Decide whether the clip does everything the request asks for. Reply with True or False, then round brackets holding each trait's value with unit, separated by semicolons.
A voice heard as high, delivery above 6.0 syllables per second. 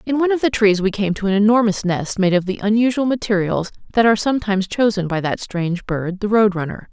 True (205 Hz; 6.3 syllables/s)